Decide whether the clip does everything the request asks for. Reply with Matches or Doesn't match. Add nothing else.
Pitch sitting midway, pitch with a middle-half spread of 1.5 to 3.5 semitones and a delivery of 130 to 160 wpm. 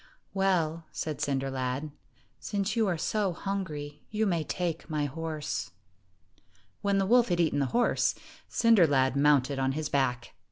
Doesn't match